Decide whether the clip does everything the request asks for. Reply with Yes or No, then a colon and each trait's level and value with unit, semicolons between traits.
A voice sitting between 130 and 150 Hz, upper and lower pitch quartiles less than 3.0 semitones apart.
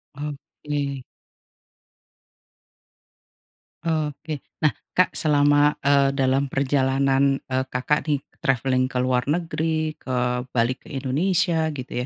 Yes: medium, 140 Hz; narrow, 2.6 semitones